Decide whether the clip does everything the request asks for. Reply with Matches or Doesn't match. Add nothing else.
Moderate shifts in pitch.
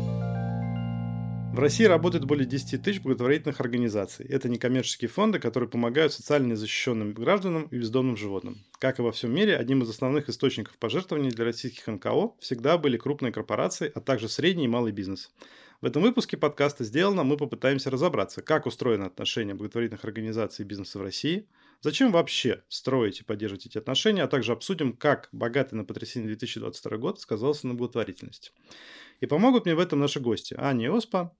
Matches